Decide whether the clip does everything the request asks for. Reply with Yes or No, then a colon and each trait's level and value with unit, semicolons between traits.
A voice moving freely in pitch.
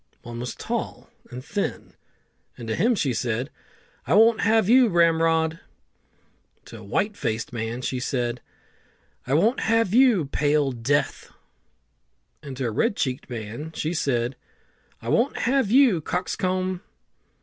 Yes: wide, 8.7 semitones